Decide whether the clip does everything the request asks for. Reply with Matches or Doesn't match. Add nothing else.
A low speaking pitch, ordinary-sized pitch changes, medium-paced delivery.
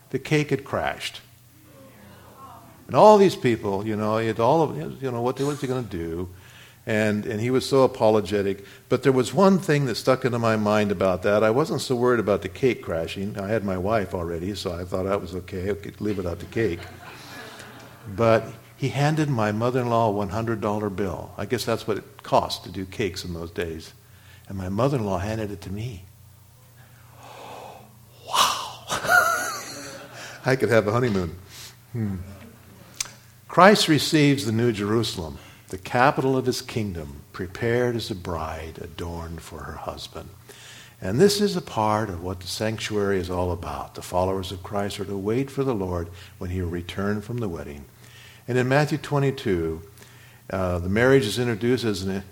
Matches